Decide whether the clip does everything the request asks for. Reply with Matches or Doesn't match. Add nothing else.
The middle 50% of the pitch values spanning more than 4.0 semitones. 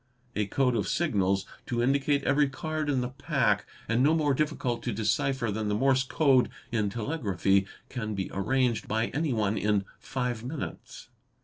Matches